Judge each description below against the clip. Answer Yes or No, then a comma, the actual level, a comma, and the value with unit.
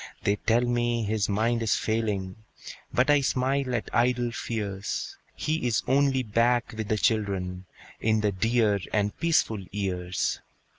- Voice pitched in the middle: No, low, 110 Hz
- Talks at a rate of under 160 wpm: Yes, average, 145 wpm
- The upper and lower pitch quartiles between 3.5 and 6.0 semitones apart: No, average, 3.1 semitones